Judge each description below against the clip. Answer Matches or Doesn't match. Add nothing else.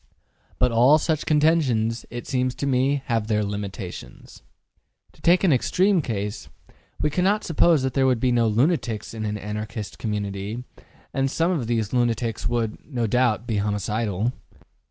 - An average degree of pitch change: Matches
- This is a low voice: Matches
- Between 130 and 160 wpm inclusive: Matches